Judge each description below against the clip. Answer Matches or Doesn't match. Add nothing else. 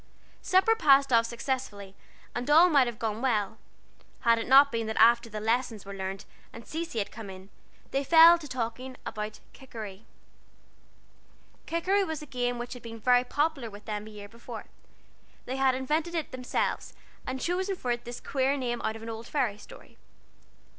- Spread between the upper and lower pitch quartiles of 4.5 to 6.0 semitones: Doesn't match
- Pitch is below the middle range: Doesn't match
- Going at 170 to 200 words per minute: Matches